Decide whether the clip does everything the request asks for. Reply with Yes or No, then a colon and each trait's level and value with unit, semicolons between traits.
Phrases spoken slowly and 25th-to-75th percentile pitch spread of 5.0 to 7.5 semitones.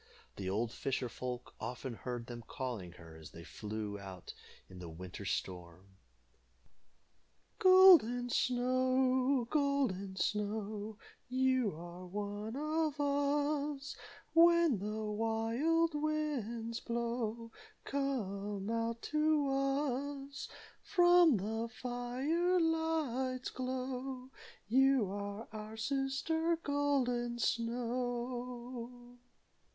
Yes: slow, 95 wpm; wide, 5.4 semitones